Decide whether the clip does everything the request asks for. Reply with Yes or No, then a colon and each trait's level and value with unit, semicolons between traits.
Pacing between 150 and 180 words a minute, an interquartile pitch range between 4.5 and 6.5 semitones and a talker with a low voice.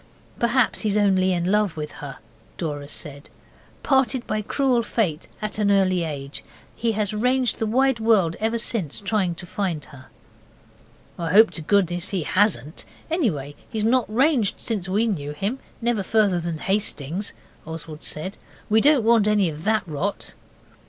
No: average, 160 wpm; average, 5.2 semitones; high, 200 Hz